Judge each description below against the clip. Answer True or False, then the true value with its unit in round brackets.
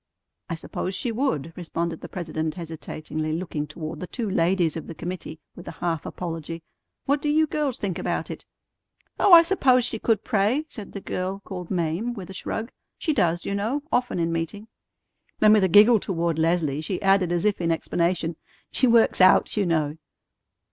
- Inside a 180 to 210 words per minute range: True (190 wpm)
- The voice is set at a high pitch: False (180 Hz)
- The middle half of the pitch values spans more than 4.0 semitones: True (4.7 semitones)